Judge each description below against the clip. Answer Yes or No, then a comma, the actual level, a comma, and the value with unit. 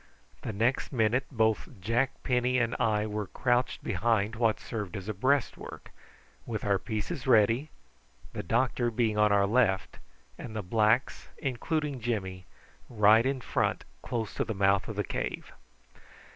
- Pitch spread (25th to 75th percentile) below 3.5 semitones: Yes, average, 2.9 semitones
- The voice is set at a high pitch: No, low, 115 Hz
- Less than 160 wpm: Yes, average, 150 wpm